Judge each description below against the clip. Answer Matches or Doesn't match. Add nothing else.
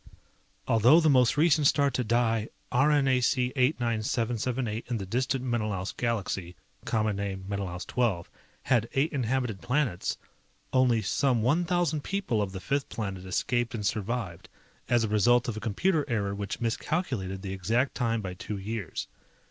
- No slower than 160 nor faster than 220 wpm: Doesn't match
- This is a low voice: Matches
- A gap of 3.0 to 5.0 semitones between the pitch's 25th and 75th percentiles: Matches